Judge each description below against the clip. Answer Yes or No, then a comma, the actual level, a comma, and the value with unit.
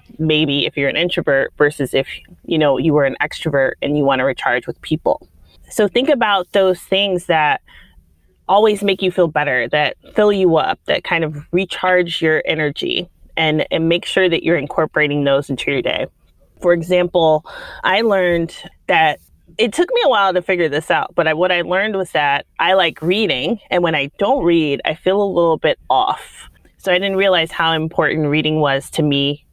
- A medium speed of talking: Yes, average, 195 wpm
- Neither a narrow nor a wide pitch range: Yes, average, 4.1 semitones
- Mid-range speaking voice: Yes, medium, 165 Hz